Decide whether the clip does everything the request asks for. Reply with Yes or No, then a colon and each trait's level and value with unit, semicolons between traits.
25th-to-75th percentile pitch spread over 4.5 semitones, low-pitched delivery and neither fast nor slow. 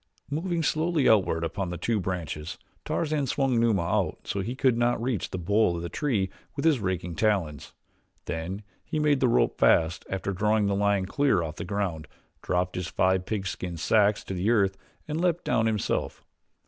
Yes: average, 5.2 semitones; low, 100 Hz; average, 185 wpm